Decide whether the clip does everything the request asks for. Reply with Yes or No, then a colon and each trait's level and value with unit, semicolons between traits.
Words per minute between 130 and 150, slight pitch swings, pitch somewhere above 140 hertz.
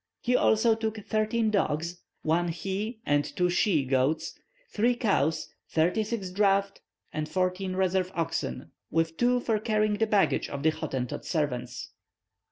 No: average, 145 wpm; average, 5.2 semitones; medium, 185 Hz